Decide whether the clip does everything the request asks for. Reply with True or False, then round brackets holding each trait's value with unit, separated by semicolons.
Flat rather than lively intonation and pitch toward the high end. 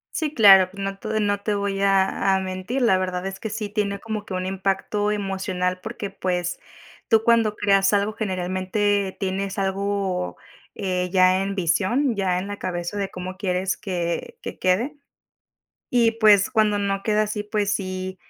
True (2.0 semitones; 195 Hz)